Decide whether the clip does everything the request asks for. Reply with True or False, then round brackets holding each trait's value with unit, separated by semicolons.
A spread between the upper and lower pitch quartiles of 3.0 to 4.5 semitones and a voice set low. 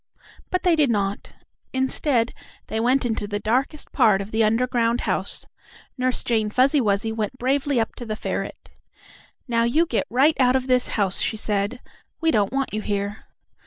False (3.5 semitones; 235 Hz)